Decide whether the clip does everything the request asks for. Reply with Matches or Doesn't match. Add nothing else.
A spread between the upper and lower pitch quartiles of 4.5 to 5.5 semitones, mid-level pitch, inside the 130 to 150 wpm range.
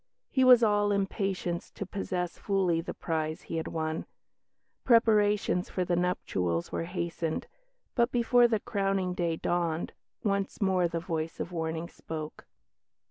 Doesn't match